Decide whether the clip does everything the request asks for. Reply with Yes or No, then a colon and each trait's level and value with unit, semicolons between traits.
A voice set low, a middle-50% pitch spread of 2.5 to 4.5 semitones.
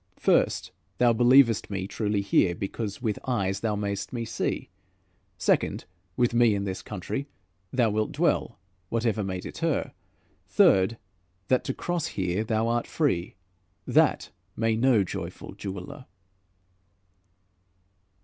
Yes: low, 110 Hz; average, 3.4 semitones